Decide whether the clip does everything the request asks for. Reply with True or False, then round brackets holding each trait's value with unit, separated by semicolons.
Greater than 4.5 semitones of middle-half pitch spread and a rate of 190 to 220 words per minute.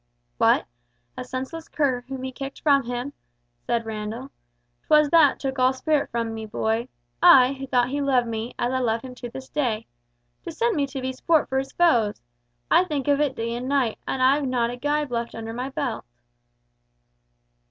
False (2.9 semitones; 195 wpm)